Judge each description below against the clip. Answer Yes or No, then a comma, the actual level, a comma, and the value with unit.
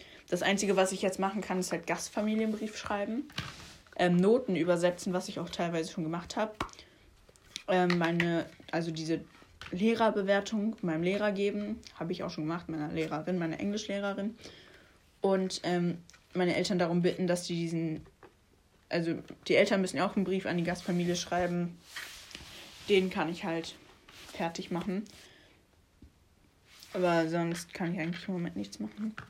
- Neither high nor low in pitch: Yes, medium, 175 Hz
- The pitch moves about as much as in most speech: Yes, average, 3.0 semitones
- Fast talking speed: No, average, 150 wpm